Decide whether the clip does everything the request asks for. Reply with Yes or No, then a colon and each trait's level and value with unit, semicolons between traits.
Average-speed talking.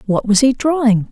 No: fast, 215 wpm